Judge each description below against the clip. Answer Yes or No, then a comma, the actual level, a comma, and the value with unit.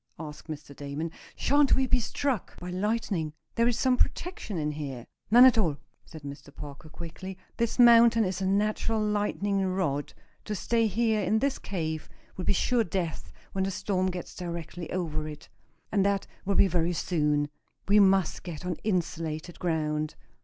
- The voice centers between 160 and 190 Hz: Yes, medium, 185 Hz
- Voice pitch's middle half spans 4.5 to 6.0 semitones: Yes, average, 5.2 semitones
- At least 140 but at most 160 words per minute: No, average, 170 wpm